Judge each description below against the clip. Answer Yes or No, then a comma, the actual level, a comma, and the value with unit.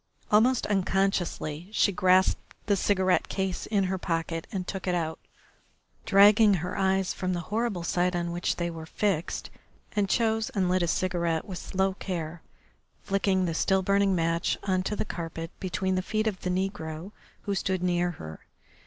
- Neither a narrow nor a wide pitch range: No, narrow, 2.3 semitones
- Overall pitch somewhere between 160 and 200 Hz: Yes, medium, 185 Hz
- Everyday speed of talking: Yes, average, 170 wpm